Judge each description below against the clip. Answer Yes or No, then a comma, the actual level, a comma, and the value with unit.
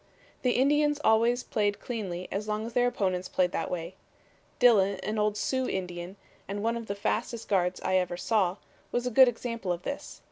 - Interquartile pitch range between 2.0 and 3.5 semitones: No, average, 4.4 semitones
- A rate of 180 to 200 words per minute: Yes, average, 190 wpm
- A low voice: No, high, 210 Hz